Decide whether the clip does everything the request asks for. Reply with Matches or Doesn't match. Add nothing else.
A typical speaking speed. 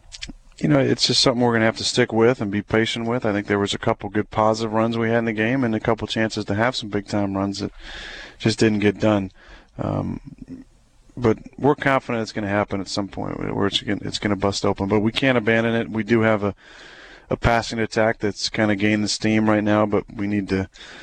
Doesn't match